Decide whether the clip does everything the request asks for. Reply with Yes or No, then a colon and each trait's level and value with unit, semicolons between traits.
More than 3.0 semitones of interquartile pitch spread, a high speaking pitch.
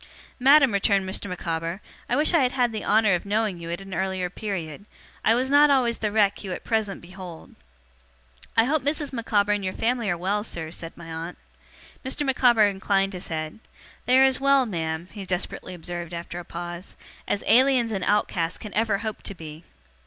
Yes: average, 5.0 semitones; high, 200 Hz